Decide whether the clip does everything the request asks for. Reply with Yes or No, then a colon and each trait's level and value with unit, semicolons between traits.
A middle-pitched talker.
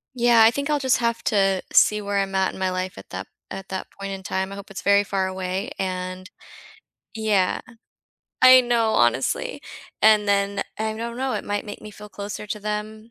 No: high, 205 Hz